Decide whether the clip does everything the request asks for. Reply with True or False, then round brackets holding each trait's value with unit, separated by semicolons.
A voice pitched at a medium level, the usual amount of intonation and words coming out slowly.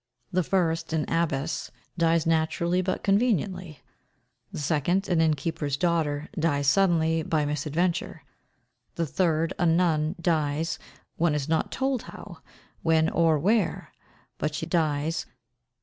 False (165 Hz; 2.2 semitones; 125 wpm)